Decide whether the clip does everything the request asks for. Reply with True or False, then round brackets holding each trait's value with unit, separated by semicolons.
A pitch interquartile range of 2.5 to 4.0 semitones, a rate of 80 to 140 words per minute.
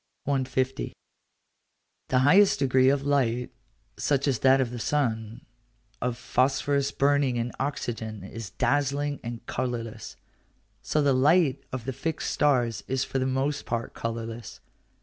True (3.0 semitones; 135 wpm)